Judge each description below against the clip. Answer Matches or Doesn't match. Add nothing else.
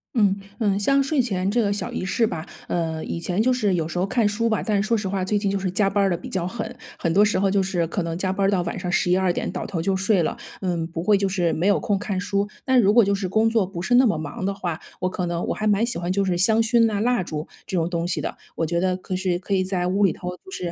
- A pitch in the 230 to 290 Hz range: Doesn't match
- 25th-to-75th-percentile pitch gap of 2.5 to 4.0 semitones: Matches